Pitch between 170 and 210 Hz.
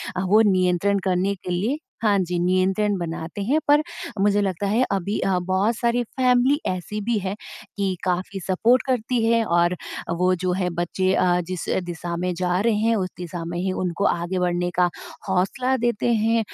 Yes: high, 190 Hz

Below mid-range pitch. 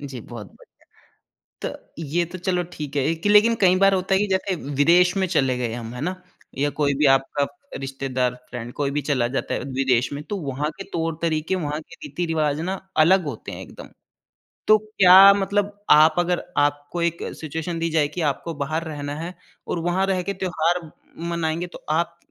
No: medium, 160 Hz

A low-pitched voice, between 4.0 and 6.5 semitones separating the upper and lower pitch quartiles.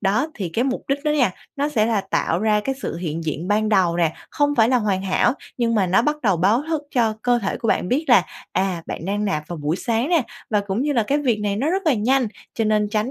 No: high, 215 Hz; average, 5.1 semitones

